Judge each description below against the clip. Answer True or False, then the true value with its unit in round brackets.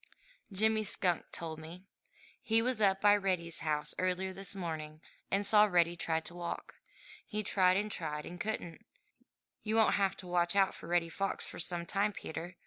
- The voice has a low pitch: False (185 Hz)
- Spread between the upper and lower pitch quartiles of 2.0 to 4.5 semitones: True (3.1 semitones)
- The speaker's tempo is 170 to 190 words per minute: True (180 wpm)